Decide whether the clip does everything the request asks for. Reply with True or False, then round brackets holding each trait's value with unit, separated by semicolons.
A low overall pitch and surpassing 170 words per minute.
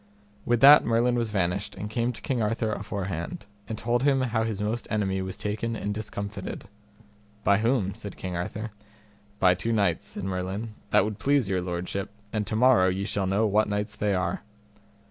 True (105 Hz; 185 wpm)